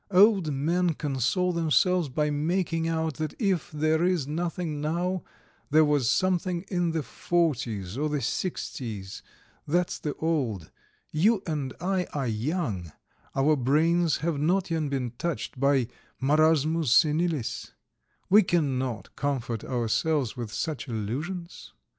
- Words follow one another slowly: Yes, slow, 130 wpm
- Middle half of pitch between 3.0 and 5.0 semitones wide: Yes, average, 4.5 semitones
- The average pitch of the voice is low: No, medium, 155 Hz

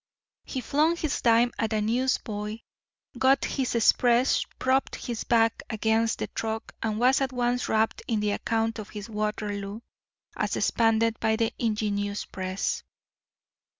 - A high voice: Yes, high, 225 Hz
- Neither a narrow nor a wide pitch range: No, narrow, 2.3 semitones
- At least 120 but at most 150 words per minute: Yes, average, 145 wpm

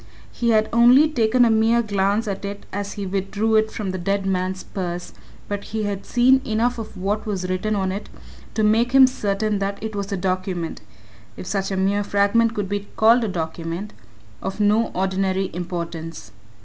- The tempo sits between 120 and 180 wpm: No, average, 190 wpm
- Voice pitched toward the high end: Yes, high, 200 Hz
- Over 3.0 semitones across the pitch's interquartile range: No, narrow, 2.5 semitones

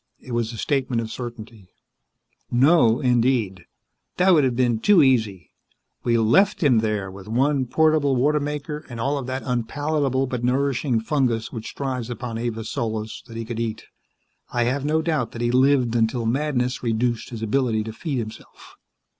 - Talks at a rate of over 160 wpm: Yes, average, 170 wpm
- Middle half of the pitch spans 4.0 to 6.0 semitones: No, average, 3.4 semitones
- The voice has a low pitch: Yes, low, 125 Hz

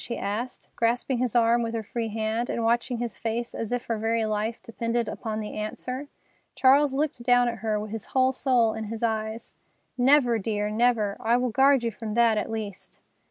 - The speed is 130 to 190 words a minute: No, average, 200 wpm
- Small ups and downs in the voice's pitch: Yes, narrow, 2.0 semitones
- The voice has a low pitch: No, high, 230 Hz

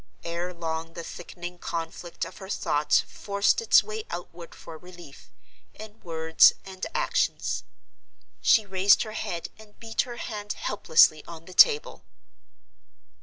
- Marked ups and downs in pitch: No, average, 3.9 semitones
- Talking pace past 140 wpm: No, slow, 135 wpm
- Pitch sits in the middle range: Yes, medium, 180 Hz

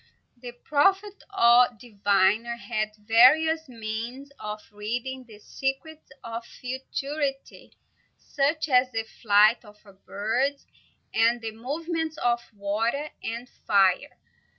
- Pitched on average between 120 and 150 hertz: No, high, 240 Hz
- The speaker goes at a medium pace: No, slow, 105 wpm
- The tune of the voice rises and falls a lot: No, average, 4.3 semitones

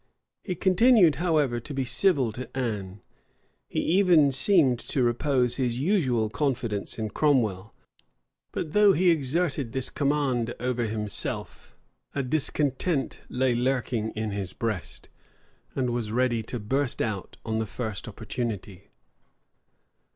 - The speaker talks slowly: Yes, slow, 130 wpm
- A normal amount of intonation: Yes, average, 4.7 semitones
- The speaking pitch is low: Yes, low, 125 Hz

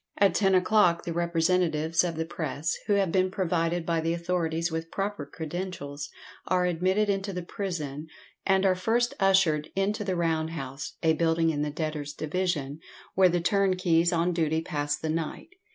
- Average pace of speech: Yes, average, 170 wpm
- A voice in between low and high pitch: Yes, medium, 170 Hz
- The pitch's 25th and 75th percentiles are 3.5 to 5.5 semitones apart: No, average, 2.7 semitones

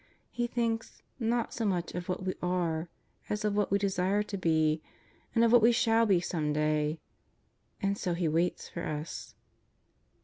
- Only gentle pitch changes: No, average, 5.2 semitones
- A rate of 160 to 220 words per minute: Yes, average, 170 wpm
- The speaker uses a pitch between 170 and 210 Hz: Yes, medium, 185 Hz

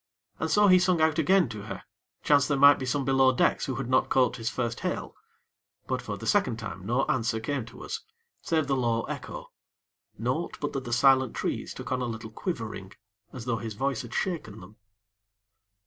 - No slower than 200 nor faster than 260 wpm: Yes, fast, 205 wpm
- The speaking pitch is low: Yes, low, 130 Hz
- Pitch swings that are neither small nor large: Yes, average, 3.9 semitones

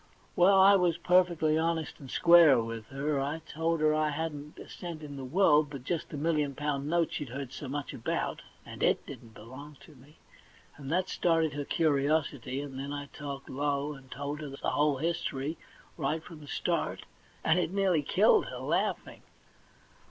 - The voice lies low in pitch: No, medium, 150 Hz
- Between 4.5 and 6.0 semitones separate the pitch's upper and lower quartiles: No, average, 2.9 semitones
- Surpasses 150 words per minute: Yes, average, 185 wpm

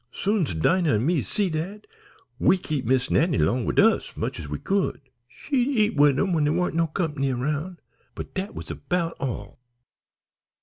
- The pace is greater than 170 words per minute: Yes, average, 180 wpm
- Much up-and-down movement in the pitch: Yes, wide, 5.7 semitones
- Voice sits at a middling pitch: Yes, medium, 160 Hz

